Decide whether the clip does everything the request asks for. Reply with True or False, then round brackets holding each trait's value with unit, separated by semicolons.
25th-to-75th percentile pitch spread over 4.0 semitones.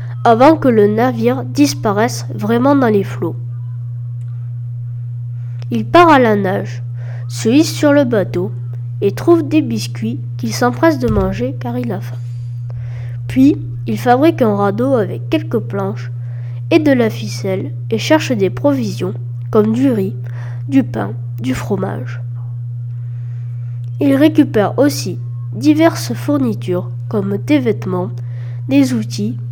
False (2.6 semitones)